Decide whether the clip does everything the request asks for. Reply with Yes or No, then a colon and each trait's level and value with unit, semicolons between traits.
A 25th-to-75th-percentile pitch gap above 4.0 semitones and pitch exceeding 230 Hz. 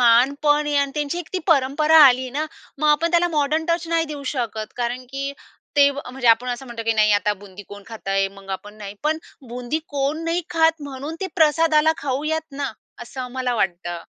Yes: average, 4.5 semitones; very high, 275 Hz